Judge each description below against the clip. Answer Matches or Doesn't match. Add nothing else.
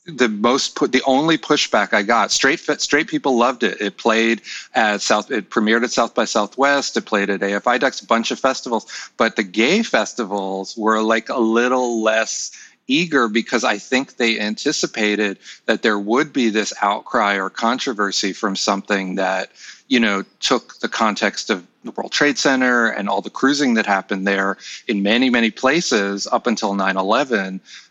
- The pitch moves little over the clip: Doesn't match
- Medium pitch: Doesn't match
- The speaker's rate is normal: Matches